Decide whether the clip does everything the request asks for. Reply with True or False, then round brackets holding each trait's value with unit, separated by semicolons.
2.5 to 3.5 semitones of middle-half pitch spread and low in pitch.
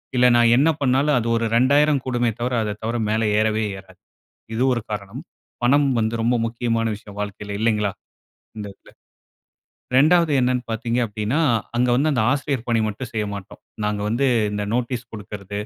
True (3.2 semitones; 115 Hz)